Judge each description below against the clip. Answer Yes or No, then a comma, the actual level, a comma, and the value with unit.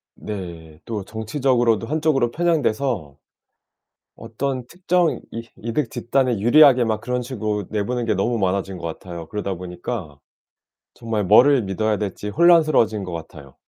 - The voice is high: No, low, 110 Hz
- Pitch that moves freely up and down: No, average, 4.8 semitones